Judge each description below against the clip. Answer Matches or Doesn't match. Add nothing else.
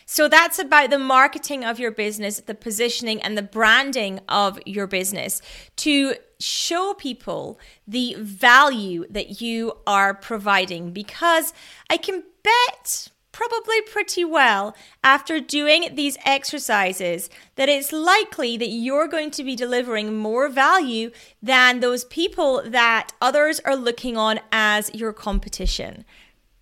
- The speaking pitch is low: Doesn't match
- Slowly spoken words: Matches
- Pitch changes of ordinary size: Doesn't match